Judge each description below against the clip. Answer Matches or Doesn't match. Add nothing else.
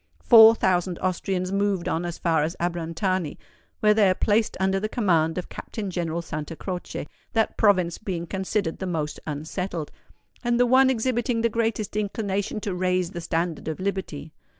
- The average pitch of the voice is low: Doesn't match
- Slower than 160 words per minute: Doesn't match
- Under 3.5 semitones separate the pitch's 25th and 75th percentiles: Doesn't match